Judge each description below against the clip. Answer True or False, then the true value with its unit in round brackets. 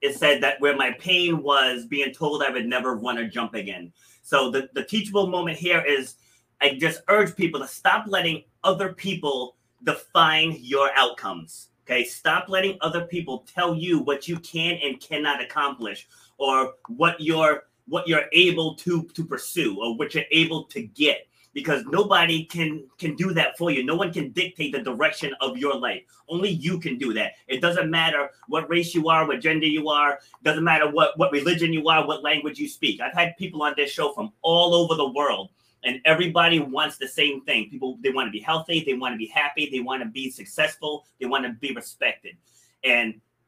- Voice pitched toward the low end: False (155 Hz)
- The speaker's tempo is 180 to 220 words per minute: True (200 wpm)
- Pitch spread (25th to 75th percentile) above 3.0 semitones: True (4.1 semitones)